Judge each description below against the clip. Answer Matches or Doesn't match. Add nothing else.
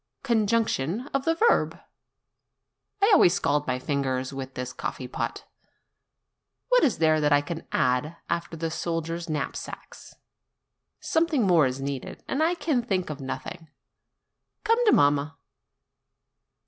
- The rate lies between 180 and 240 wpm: Doesn't match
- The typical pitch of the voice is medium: Matches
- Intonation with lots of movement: Matches